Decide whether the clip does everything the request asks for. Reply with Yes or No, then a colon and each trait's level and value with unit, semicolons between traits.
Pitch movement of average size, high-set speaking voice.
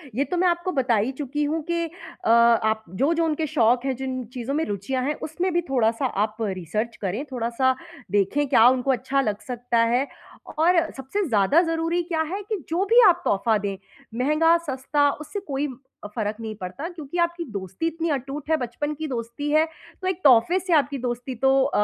No: wide, 5.7 semitones; very high, 270 Hz